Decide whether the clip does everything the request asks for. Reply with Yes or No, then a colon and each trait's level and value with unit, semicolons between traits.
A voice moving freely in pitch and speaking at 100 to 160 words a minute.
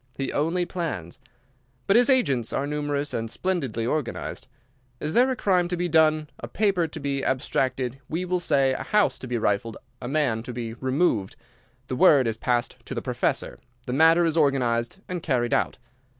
No: wide, 6.0 semitones; average, 180 wpm